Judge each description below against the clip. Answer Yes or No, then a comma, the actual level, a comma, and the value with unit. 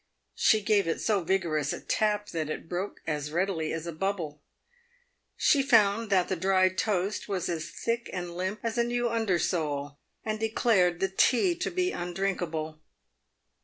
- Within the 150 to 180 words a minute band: Yes, average, 165 wpm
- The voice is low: No, high, 190 Hz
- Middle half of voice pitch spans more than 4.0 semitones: Yes, average, 4.4 semitones